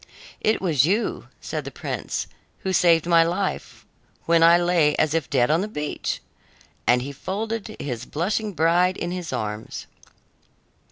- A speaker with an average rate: Yes, average, 155 wpm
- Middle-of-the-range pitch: Yes, medium, 170 Hz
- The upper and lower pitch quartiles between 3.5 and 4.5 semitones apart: Yes, average, 4.0 semitones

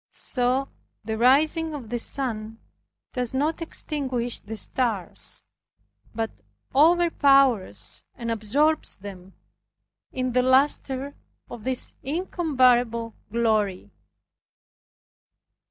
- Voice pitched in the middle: No, very high, 250 Hz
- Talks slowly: Yes, slow, 90 wpm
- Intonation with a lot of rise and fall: No, average, 3.8 semitones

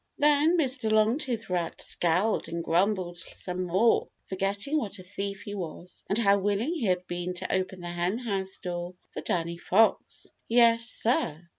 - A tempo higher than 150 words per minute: Yes, average, 160 wpm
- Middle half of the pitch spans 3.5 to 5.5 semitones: Yes, average, 4.2 semitones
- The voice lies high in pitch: Yes, high, 195 Hz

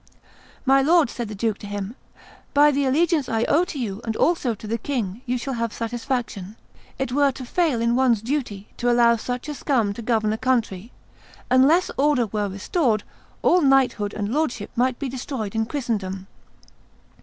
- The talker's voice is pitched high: Yes, high, 240 Hz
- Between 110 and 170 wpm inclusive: No, average, 180 wpm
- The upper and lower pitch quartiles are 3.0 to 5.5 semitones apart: Yes, average, 4.0 semitones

